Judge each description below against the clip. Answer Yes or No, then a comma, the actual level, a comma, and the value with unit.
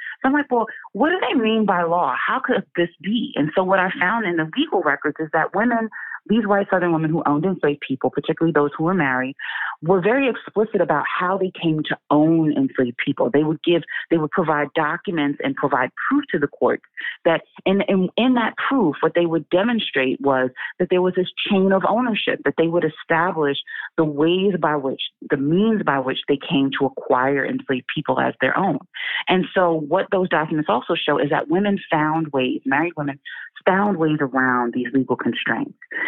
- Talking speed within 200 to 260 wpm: Yes, fast, 205 wpm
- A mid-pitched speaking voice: Yes, medium, 165 Hz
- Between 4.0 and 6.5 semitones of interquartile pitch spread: Yes, average, 4.9 semitones